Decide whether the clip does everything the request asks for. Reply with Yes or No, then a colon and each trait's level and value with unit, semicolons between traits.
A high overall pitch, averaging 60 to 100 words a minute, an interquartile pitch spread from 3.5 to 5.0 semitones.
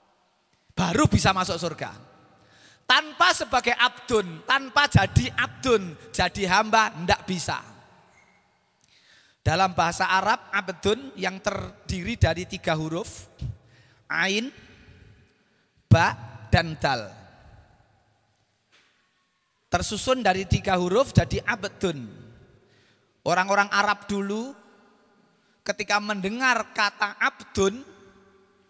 Yes: high, 195 Hz; slow, 85 wpm; average, 3.8 semitones